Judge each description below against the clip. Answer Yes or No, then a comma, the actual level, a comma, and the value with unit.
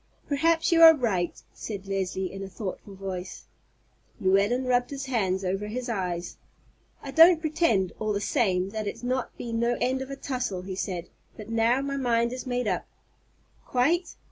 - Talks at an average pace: Yes, average, 175 wpm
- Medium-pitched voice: No, high, 230 Hz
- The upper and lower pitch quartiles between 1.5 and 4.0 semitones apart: No, average, 5.3 semitones